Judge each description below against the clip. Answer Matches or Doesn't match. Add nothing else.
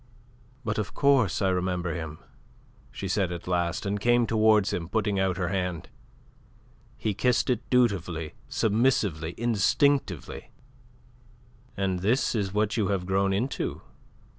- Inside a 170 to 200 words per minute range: Doesn't match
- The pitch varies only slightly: Doesn't match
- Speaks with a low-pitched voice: Matches